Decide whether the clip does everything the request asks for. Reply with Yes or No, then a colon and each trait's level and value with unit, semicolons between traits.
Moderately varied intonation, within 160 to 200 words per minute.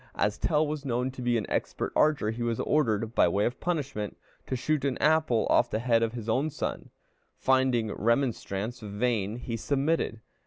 Yes: average, 3.9 semitones; average, 185 wpm